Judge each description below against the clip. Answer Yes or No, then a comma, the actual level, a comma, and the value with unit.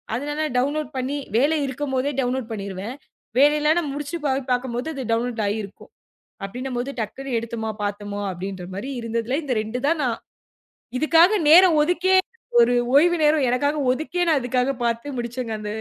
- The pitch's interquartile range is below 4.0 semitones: No, average, 4.3 semitones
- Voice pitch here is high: Yes, very high, 255 Hz